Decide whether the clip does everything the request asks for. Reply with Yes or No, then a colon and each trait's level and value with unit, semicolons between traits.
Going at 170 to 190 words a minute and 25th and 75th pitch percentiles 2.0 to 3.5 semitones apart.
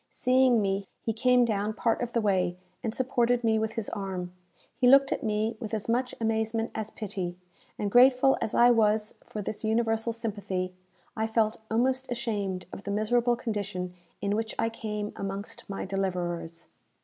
Yes: average, 175 wpm; average, 2.8 semitones